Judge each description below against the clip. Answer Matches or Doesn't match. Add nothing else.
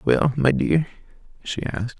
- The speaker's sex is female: Doesn't match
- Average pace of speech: Matches